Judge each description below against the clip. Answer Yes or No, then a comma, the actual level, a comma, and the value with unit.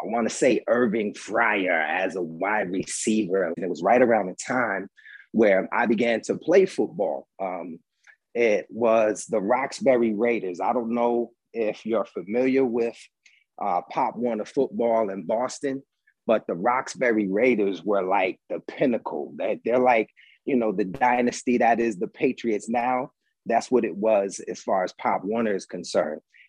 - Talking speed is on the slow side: No, average, 165 wpm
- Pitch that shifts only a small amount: Yes, narrow, 2.3 semitones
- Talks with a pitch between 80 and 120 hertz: Yes, low, 115 Hz